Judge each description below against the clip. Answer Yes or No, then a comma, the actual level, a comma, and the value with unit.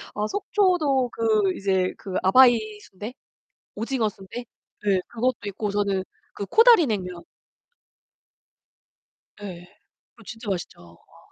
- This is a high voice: Yes, high, 215 Hz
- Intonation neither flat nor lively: Yes, average, 4.6 semitones